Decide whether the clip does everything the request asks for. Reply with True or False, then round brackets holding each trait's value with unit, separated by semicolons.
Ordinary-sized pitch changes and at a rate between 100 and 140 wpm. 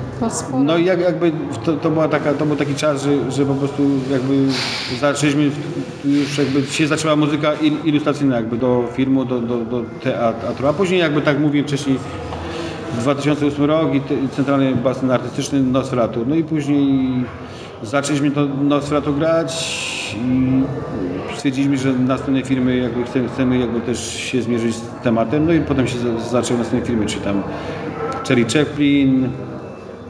False (3.1 semitones; 155 wpm)